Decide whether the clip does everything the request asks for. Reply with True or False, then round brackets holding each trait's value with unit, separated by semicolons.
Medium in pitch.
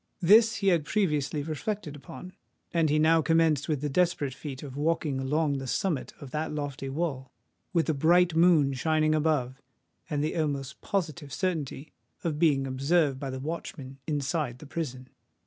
True (150 Hz)